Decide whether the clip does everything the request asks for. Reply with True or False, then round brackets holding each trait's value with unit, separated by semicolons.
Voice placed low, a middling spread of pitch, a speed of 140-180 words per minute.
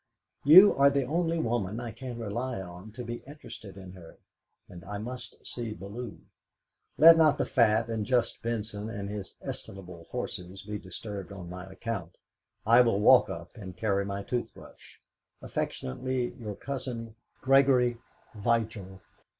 True (110 Hz; 3.9 semitones; 150 wpm)